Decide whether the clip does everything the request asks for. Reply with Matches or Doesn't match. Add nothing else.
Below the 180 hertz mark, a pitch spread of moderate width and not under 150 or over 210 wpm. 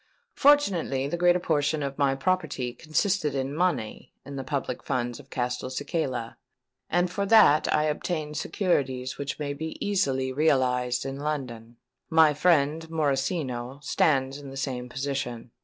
Doesn't match